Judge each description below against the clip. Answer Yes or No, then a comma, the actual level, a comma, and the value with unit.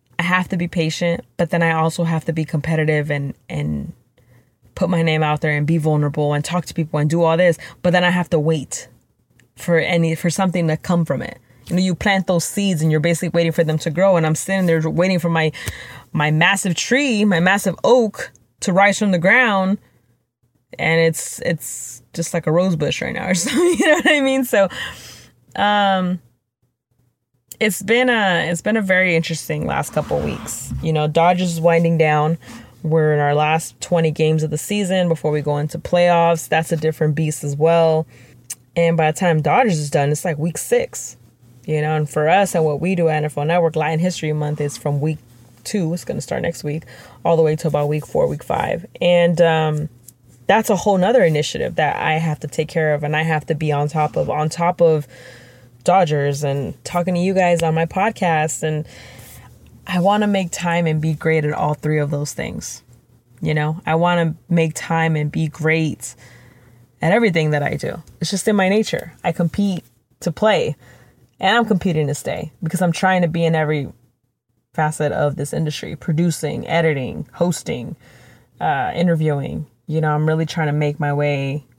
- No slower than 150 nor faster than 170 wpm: No, fast, 205 wpm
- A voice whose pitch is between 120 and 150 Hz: No, medium, 160 Hz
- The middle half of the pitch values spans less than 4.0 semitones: Yes, average, 2.9 semitones